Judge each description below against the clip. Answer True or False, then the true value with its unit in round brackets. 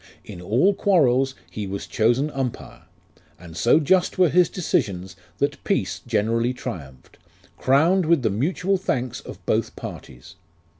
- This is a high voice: False (130 Hz)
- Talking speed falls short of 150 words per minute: True (140 wpm)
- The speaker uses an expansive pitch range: True (8.0 semitones)